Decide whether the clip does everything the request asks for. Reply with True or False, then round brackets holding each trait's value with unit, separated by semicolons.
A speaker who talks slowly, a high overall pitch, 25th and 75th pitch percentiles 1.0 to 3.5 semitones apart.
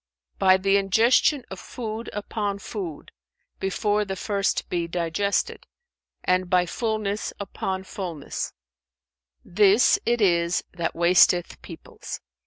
True (110 wpm; 195 Hz; 2.8 semitones)